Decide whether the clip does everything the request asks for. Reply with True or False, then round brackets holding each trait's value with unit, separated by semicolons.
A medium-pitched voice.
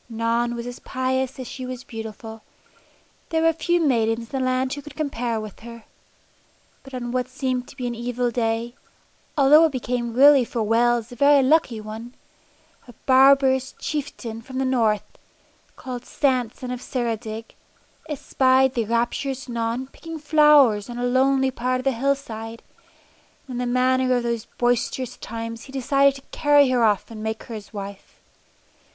False (250 Hz)